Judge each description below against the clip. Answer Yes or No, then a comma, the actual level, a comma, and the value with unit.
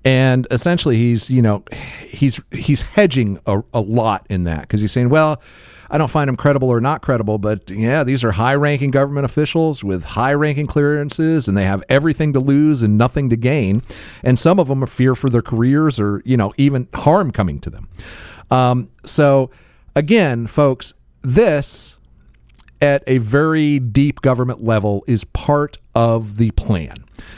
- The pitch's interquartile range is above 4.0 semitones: Yes, average, 5.1 semitones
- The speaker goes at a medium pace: Yes, average, 175 wpm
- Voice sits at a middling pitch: No, low, 125 Hz